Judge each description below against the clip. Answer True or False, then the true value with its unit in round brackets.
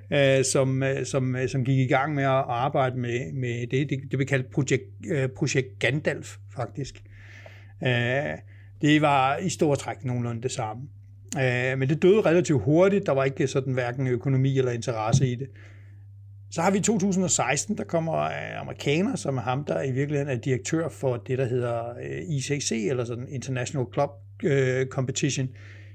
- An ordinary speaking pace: True (175 wpm)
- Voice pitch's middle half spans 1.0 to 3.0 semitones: True (2.7 semitones)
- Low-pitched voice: True (130 Hz)